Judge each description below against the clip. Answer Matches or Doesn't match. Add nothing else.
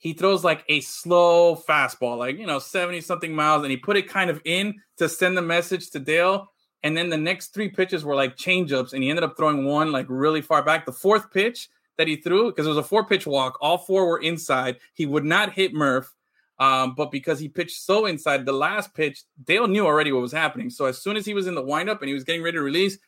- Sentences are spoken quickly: Matches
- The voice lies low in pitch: Doesn't match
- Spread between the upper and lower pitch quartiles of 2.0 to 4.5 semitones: Matches